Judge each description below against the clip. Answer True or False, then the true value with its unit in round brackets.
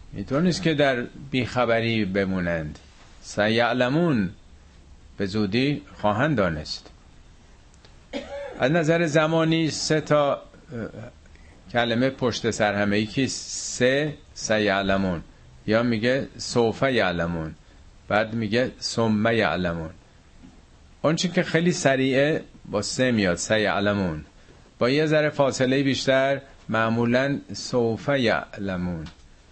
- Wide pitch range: True (6.5 semitones)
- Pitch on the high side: False (115 Hz)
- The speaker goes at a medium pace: False (100 wpm)